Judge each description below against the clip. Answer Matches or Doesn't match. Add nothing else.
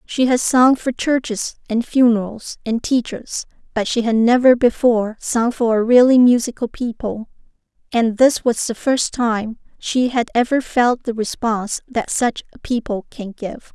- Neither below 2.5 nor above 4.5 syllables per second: Matches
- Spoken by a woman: Matches